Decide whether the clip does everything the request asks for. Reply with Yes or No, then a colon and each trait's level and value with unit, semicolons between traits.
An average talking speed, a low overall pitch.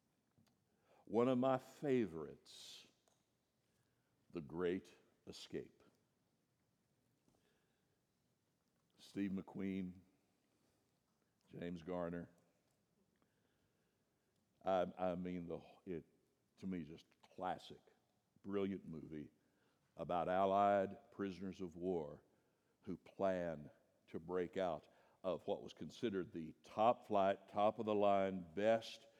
No: slow, 90 wpm; very low, 95 Hz